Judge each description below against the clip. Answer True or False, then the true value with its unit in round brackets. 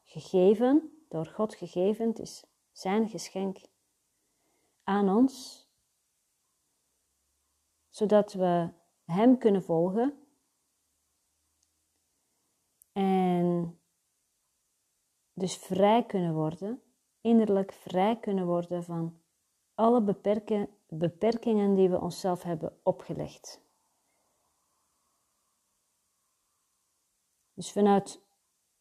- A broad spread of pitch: False (4.1 semitones)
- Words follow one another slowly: True (75 wpm)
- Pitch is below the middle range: False (190 Hz)